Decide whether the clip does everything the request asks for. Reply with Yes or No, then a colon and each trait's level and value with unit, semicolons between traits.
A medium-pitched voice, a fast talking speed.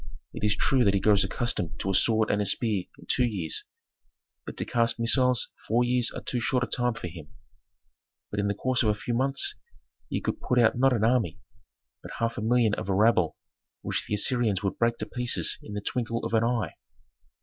No: low, 115 Hz; fast, 220 wpm